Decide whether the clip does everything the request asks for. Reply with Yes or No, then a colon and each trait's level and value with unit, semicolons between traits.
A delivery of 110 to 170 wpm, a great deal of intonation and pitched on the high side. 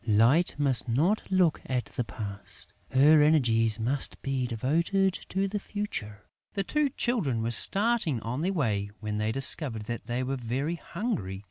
No: average, 160 wpm; wide, 7.6 semitones; low, 135 Hz